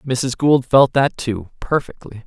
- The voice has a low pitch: Yes, low, 130 Hz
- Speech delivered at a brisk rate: No, average, 160 wpm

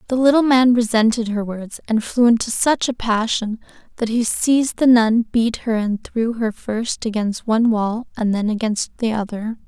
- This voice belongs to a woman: Yes, female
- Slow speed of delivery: No, average, 190 wpm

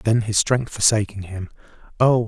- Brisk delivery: No, average, 160 wpm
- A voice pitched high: No, low, 110 Hz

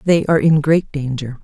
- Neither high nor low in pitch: Yes, medium, 150 Hz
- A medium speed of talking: No, fast, 210 wpm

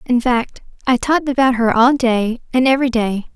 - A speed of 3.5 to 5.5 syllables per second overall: Yes, 5.4 syllables/s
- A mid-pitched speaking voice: No, high, 245 Hz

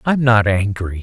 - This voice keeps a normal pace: No, fast, 235 wpm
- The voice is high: No, low, 110 Hz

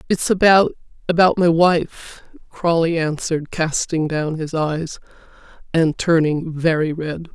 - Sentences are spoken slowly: Yes, slow, 115 wpm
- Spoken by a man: No, female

